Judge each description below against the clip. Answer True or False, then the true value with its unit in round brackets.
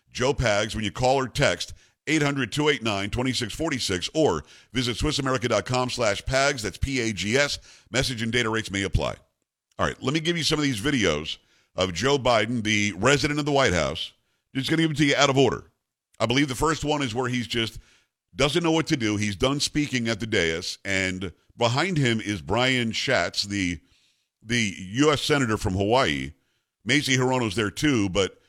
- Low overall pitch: True (125 Hz)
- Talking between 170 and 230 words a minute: True (195 wpm)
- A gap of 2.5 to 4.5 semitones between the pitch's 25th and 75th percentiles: False (5.2 semitones)